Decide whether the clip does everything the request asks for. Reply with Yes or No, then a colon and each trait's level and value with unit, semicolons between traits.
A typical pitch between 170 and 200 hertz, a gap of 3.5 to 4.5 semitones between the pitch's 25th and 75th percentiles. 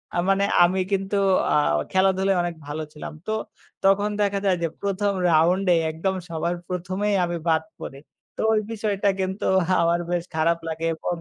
No: medium, 185 Hz; average, 2.7 semitones